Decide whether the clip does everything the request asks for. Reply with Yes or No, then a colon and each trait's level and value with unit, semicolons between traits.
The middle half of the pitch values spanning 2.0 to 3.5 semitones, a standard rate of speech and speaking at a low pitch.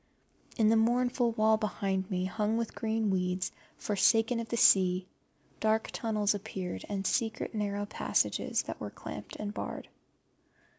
No: narrow, 2.5 semitones; average, 145 wpm; high, 215 Hz